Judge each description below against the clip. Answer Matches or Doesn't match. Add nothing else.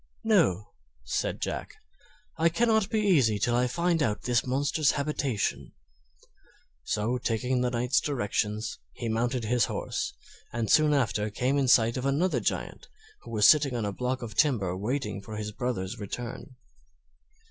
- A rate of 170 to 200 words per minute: Doesn't match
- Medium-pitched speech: Doesn't match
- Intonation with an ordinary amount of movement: Matches